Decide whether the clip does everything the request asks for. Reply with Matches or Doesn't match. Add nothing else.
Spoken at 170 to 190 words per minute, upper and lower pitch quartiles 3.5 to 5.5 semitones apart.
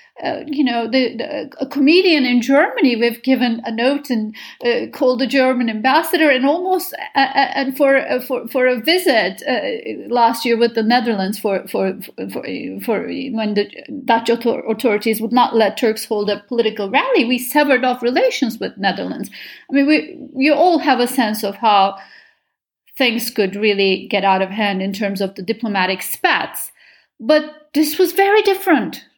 Matches